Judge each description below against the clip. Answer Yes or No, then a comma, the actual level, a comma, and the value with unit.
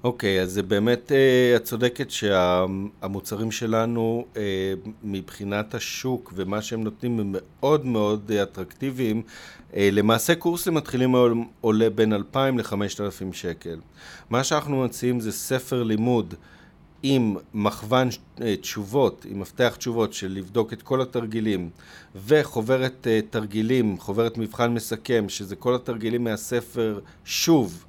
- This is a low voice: Yes, low, 110 Hz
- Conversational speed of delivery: Yes, average, 130 wpm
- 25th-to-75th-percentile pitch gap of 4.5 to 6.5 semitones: No, average, 3.7 semitones